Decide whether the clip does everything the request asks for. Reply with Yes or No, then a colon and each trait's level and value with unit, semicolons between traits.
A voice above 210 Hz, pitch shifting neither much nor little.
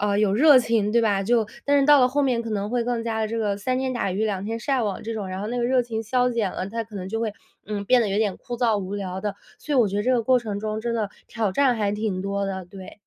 Yes: high, 220 Hz; average, 3.1 semitones